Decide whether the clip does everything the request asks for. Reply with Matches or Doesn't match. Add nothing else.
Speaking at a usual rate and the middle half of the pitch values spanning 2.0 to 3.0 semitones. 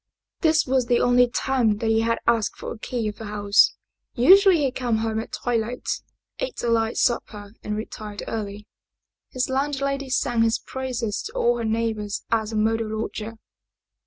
Matches